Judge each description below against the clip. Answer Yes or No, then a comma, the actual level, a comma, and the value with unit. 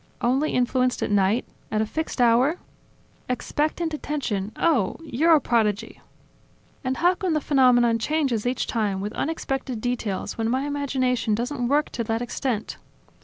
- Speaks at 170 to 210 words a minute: No, average, 150 wpm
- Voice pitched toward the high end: Yes, very high, 250 Hz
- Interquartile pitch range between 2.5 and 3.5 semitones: No, average, 4.2 semitones